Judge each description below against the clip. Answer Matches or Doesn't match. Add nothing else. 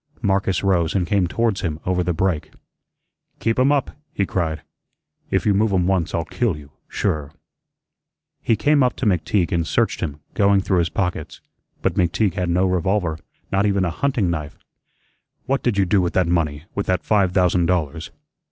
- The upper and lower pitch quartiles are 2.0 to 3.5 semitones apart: Matches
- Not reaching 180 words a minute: Doesn't match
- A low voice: Matches